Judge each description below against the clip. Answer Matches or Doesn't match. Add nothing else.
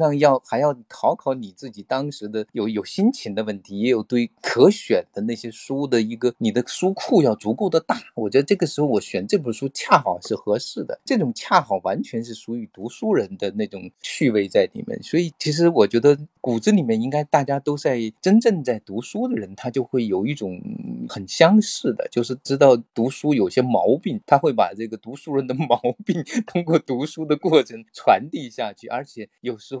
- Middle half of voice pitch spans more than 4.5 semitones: Matches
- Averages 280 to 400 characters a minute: Matches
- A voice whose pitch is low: Matches